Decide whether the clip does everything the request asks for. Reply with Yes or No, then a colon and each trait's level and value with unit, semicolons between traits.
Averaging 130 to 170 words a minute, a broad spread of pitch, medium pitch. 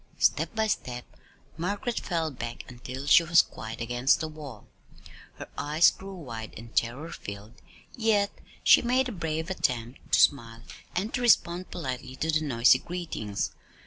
Yes: average, 155 wpm; wide, 6.9 semitones; medium, 155 Hz